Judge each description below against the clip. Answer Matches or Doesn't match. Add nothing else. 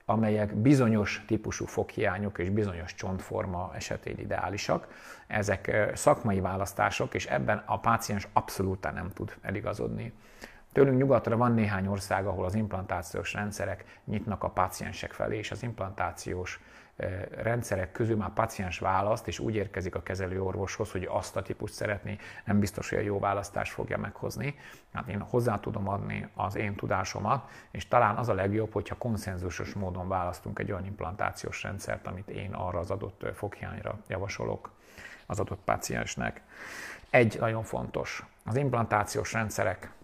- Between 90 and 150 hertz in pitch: Matches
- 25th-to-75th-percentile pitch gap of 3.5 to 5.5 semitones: Doesn't match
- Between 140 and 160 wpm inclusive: Matches